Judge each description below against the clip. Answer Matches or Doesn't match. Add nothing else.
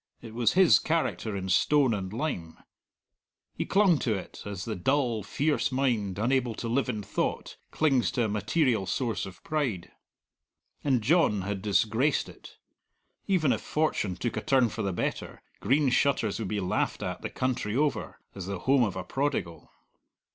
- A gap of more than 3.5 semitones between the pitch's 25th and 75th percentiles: Matches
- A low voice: Matches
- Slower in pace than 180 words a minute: Matches